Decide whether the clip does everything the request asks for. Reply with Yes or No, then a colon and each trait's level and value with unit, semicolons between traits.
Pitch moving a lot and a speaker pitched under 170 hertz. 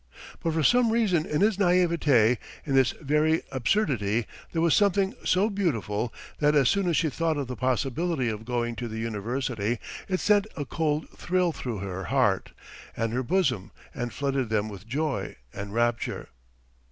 Yes: wide, 6.4 semitones; medium, 140 Hz